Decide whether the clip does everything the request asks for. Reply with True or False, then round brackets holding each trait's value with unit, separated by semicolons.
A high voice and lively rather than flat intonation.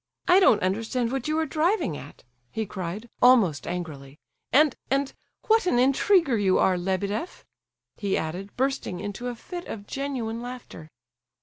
True (230 Hz; 6.4 semitones)